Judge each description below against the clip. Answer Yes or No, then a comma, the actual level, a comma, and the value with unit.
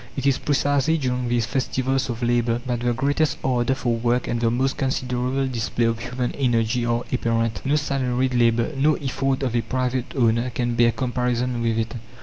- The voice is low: Yes, low, 125 Hz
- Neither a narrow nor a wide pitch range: No, narrow, 2.0 semitones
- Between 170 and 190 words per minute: Yes, average, 185 wpm